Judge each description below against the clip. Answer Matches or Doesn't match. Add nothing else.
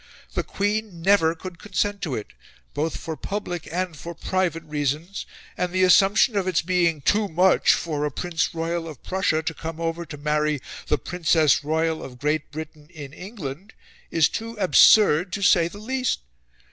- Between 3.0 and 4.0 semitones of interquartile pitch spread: Matches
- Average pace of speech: Matches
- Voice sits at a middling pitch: Matches